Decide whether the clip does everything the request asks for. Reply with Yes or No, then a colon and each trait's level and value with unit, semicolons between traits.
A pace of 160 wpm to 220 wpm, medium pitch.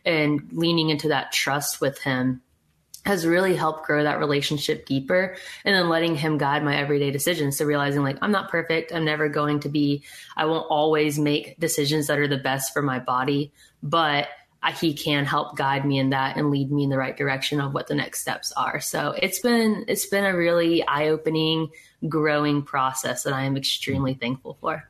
Yes: average, 200 wpm; medium, 150 Hz